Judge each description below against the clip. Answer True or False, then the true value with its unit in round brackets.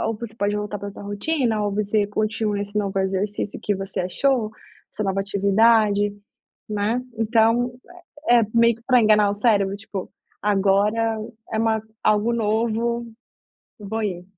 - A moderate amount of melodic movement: False (2.0 semitones)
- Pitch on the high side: True (210 Hz)